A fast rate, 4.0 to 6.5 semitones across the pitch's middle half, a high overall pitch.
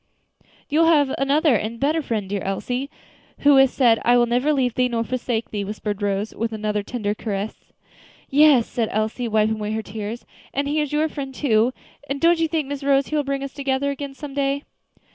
Yes: fast, 210 wpm; average, 4.4 semitones; very high, 255 Hz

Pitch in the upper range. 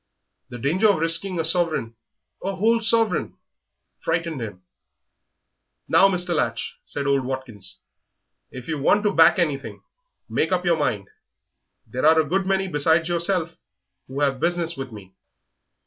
No: medium, 165 Hz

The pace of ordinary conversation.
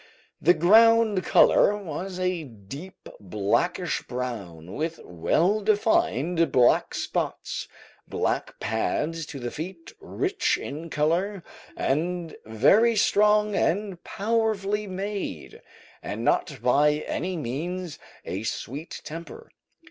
No: slow, 105 wpm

